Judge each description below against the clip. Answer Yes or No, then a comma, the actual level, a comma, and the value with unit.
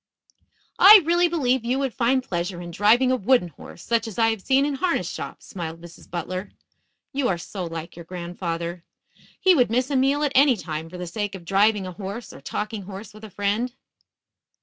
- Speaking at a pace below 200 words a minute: No, fast, 205 wpm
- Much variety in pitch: Yes, wide, 6.5 semitones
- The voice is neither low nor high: No, high, 210 Hz